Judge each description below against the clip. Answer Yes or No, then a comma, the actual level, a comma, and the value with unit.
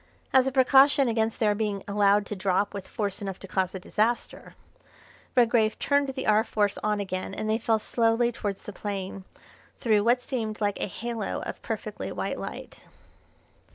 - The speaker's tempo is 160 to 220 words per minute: Yes, average, 175 wpm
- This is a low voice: No, high, 215 Hz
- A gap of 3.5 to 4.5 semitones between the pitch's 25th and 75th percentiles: No, average, 2.8 semitones